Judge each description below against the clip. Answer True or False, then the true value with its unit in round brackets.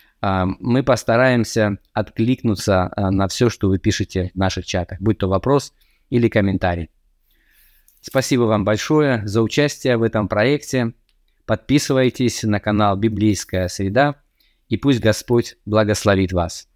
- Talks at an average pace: True (120 wpm)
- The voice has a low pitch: True (110 Hz)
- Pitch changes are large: False (4.2 semitones)